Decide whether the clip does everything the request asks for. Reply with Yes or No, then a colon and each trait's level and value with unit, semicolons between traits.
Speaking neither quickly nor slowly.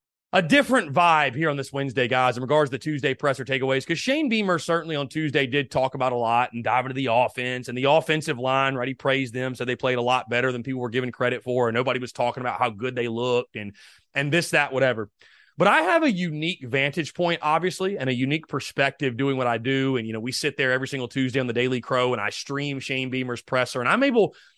No: fast, 250 wpm